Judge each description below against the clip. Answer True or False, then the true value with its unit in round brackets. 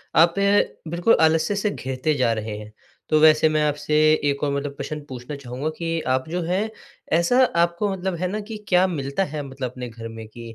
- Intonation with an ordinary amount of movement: True (5.0 semitones)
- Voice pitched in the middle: True (155 Hz)